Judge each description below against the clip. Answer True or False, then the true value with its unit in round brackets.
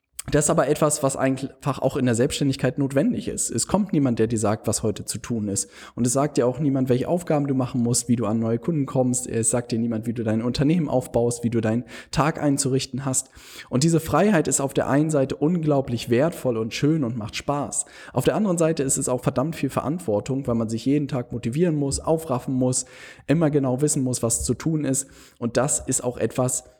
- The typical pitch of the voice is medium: False (130 Hz)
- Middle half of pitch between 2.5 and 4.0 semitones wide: True (3.4 semitones)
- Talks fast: True (230 wpm)